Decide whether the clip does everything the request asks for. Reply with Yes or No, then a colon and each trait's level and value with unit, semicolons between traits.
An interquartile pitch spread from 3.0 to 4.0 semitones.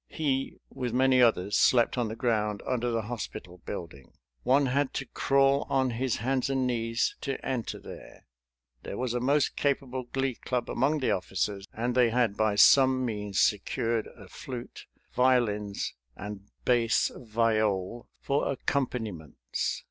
Yes: average, 3.6 semitones